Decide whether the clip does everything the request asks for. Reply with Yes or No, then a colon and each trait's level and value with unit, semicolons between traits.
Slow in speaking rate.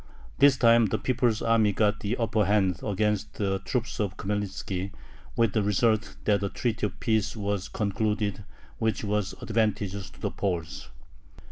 No: average, 155 wpm